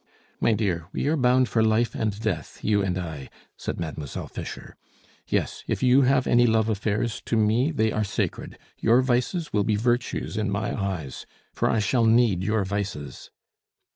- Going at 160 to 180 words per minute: Yes, average, 175 wpm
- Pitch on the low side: Yes, low, 110 Hz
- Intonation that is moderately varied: Yes, average, 3.5 semitones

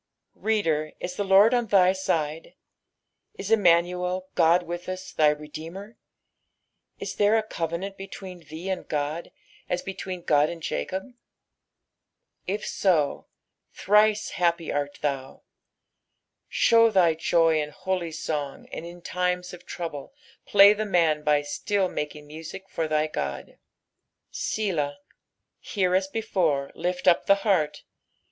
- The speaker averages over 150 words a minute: No, slow, 135 wpm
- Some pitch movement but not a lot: Yes, average, 3.9 semitones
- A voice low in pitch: No, medium, 175 Hz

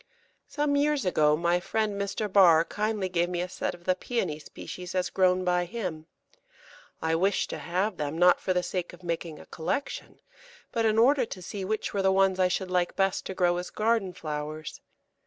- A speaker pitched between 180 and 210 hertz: Yes, medium, 185 Hz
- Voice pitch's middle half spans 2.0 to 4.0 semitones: Yes, average, 2.8 semitones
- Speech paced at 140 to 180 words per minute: No, average, 200 wpm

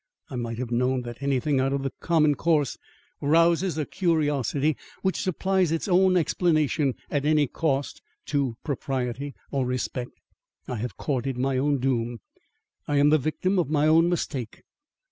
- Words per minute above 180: No, average, 160 wpm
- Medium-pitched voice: Yes, medium, 145 Hz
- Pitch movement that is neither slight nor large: Yes, average, 3.7 semitones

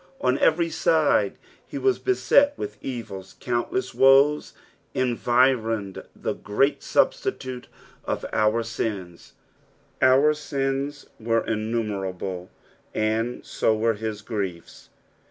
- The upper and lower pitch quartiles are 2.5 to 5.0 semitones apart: Yes, average, 4.3 semitones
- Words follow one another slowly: Yes, slow, 100 wpm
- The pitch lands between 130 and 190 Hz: No, low, 120 Hz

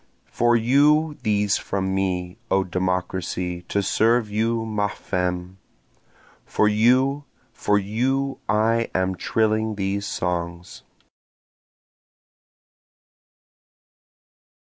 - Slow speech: Yes, slow, 85 wpm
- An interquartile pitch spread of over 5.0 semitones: No, average, 3.7 semitones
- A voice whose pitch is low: Yes, low, 105 Hz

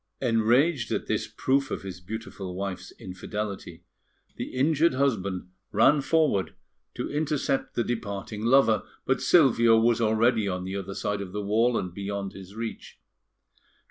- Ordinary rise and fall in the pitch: Yes, average, 4.7 semitones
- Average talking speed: Yes, average, 145 wpm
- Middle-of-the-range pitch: No, low, 110 Hz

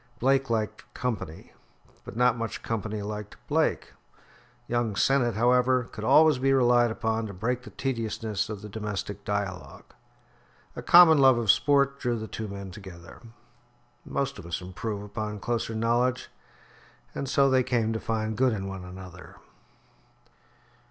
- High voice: No, low, 115 Hz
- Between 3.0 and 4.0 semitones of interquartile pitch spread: Yes, average, 3.5 semitones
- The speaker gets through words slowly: No, average, 150 wpm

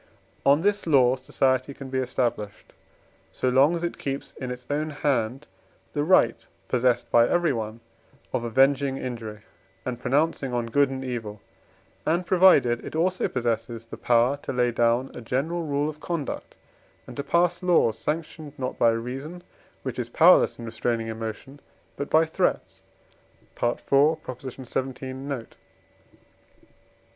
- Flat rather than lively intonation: No, average, 3.9 semitones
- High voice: No, low, 130 Hz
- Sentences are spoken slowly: No, average, 145 wpm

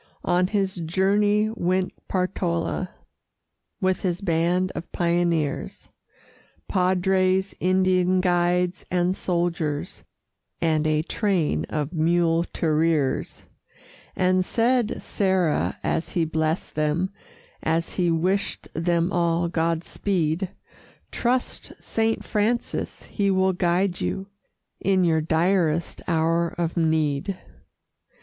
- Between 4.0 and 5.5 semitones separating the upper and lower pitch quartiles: No, narrow, 2.4 semitones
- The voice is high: No, medium, 175 Hz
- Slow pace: Yes, slow, 100 wpm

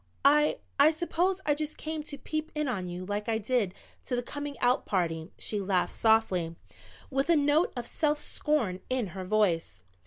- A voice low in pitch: No, high, 245 Hz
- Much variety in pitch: Yes, wide, 7.8 semitones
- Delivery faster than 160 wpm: Yes, average, 185 wpm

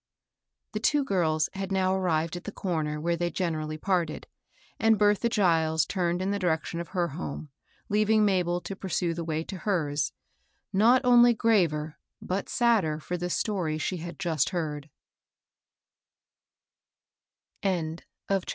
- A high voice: No, medium, 175 Hz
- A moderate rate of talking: Yes, average, 150 wpm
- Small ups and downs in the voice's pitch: No, average, 3.8 semitones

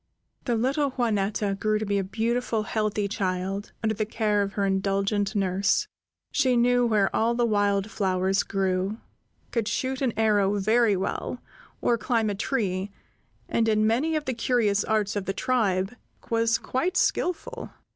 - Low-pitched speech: No, high, 215 Hz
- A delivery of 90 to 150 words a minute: No, average, 160 wpm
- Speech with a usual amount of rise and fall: Yes, average, 3.0 semitones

